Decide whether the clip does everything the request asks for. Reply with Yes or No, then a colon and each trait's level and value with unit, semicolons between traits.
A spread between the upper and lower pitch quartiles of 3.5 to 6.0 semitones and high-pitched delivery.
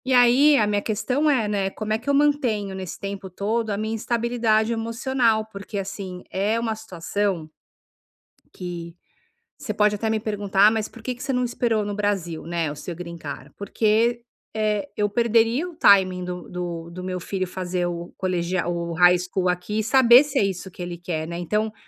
Yes: average, 3.9 semitones; high, 205 Hz